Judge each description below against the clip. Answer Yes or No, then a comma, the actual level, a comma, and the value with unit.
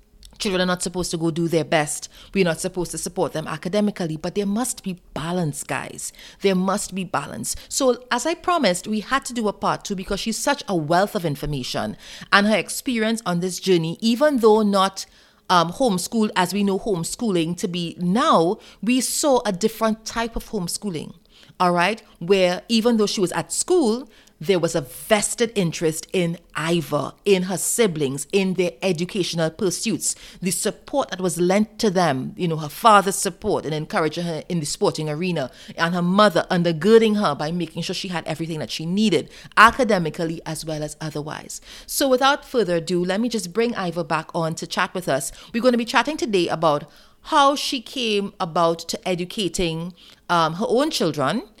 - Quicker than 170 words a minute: Yes, average, 185 wpm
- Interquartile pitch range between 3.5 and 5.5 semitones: Yes, average, 4.5 semitones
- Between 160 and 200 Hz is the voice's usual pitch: Yes, medium, 185 Hz